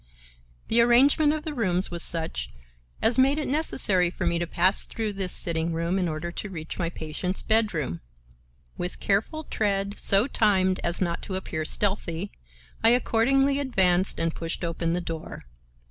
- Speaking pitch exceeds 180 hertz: Yes, high, 190 Hz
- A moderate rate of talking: Yes, average, 165 wpm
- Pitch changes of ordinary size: Yes, average, 5.0 semitones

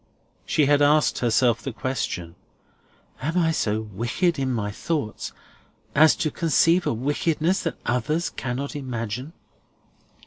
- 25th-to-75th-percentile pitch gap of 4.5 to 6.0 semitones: Yes, average, 5.1 semitones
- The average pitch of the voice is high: No, low, 135 Hz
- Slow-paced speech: Yes, slow, 130 wpm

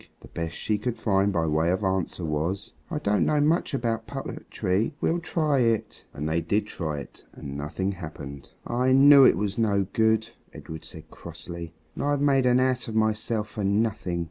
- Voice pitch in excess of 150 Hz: No, low, 105 Hz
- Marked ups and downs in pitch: Yes, wide, 6.6 semitones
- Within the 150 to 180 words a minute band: No, average, 190 wpm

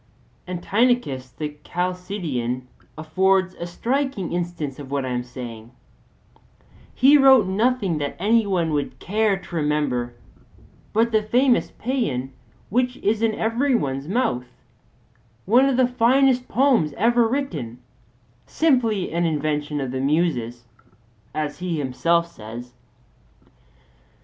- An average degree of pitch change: No, wide, 8.5 semitones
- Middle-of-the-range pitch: Yes, medium, 180 Hz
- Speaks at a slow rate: Yes, slow, 125 wpm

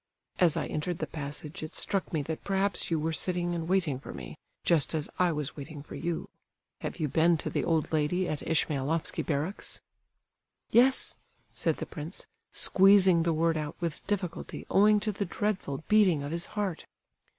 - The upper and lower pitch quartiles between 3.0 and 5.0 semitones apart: Yes, average, 3.5 semitones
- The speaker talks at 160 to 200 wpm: Yes, average, 180 wpm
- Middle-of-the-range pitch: Yes, medium, 165 Hz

